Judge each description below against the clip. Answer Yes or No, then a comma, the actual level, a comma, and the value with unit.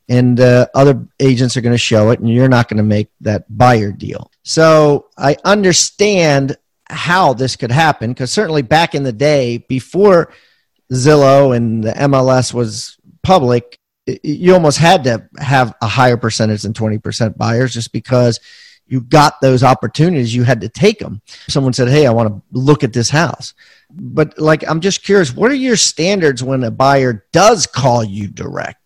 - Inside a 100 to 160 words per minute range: No, average, 180 wpm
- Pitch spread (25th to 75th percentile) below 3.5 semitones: No, average, 4.2 semitones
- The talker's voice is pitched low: Yes, low, 130 Hz